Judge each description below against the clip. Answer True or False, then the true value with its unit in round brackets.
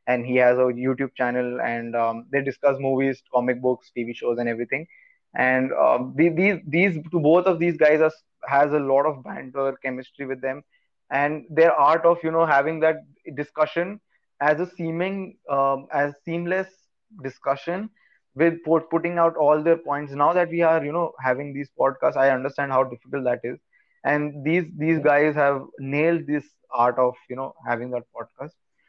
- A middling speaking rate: True (175 wpm)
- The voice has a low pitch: False (145 Hz)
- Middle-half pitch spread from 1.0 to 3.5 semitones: False (4.1 semitones)